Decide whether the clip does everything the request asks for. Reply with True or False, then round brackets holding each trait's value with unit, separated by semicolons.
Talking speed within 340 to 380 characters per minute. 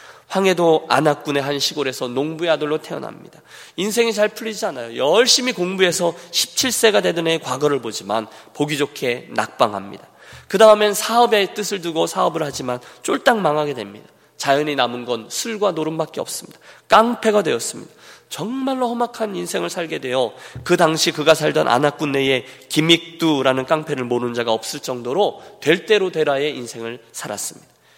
True (360 characters per minute)